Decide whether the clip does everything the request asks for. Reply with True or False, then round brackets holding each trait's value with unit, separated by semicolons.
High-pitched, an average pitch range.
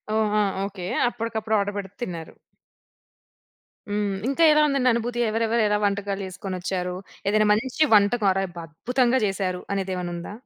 True (205 Hz; 3.1 semitones)